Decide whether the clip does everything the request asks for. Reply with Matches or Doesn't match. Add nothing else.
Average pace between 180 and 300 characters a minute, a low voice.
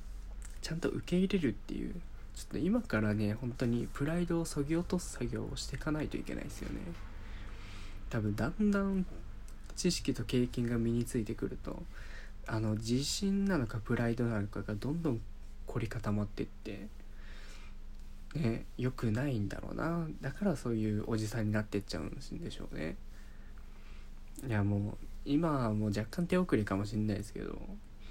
Doesn't match